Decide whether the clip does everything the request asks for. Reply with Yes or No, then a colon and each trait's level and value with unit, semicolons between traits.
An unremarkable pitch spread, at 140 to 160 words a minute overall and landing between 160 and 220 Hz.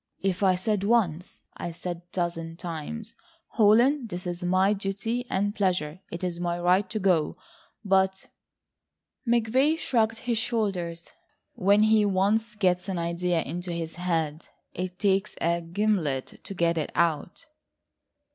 Yes: average, 3.6 semitones; average, 145 wpm; medium, 185 Hz